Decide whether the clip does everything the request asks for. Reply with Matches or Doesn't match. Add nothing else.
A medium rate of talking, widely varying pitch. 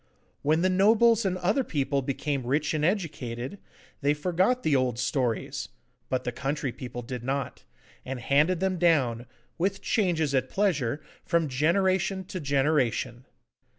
Matches